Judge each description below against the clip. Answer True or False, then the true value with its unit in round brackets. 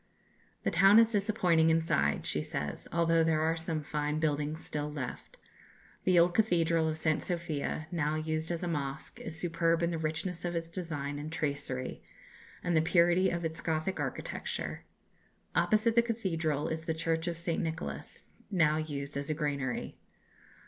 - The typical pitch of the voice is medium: True (160 Hz)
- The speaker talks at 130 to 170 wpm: True (165 wpm)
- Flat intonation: True (2.1 semitones)